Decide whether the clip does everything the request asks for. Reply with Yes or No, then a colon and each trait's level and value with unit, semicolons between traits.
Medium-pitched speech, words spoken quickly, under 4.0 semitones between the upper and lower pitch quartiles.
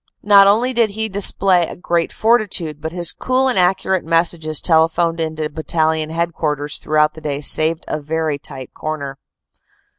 No: medium, 165 Hz; average, 155 wpm; average, 3.5 semitones